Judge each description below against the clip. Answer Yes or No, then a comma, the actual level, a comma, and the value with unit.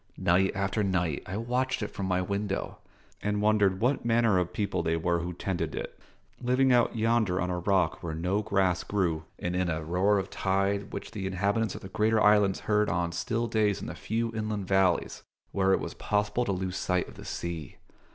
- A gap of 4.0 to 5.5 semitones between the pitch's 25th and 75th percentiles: No, average, 2.9 semitones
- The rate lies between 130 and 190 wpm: No, fast, 205 wpm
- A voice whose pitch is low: Yes, low, 100 Hz